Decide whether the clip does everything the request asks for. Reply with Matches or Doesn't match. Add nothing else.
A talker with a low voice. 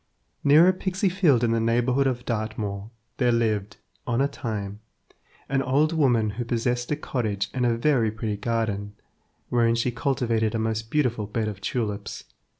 Matches